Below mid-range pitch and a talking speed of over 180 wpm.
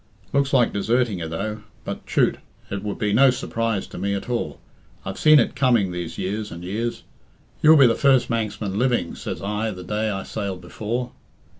Yes: low, 110 Hz; average, 190 wpm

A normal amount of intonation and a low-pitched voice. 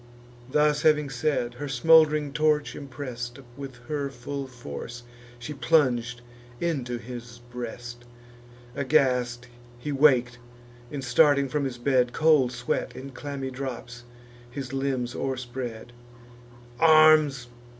Yes: average, 3.2 semitones; low, 130 Hz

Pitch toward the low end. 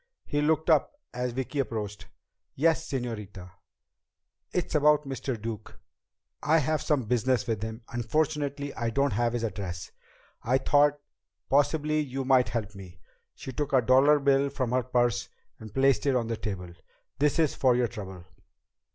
Yes: low, 130 Hz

